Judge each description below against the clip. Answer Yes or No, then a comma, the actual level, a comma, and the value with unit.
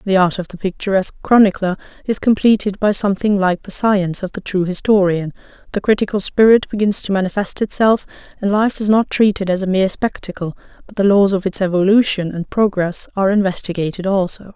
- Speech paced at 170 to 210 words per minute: Yes, average, 180 wpm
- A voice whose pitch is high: Yes, high, 195 Hz